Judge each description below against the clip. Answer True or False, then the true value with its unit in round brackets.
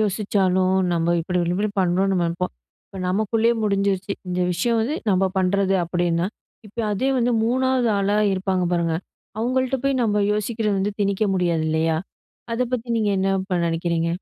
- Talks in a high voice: True (195 Hz)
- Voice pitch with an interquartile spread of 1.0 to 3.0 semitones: False (3.6 semitones)